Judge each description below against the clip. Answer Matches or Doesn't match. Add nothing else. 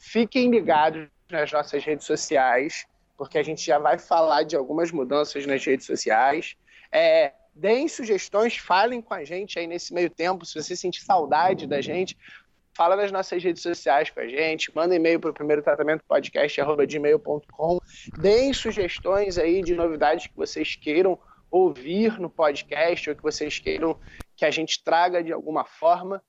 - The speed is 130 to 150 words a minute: Doesn't match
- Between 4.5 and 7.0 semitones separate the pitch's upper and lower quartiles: Matches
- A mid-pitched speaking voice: Matches